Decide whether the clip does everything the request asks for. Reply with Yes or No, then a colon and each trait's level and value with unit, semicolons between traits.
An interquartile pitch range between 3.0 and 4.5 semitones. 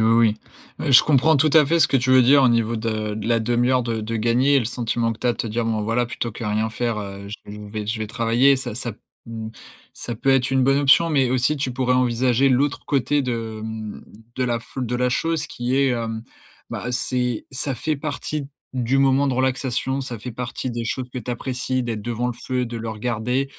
No: narrow, 2.6 semitones